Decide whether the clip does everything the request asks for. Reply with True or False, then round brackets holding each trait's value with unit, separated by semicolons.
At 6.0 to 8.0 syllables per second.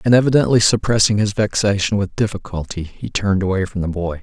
True (6.1 syllables/s)